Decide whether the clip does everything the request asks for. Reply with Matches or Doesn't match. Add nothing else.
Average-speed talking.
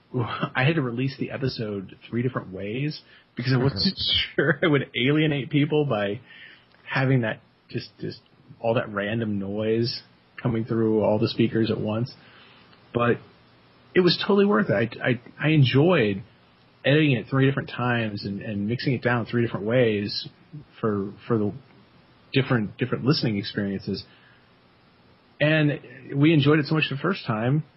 Matches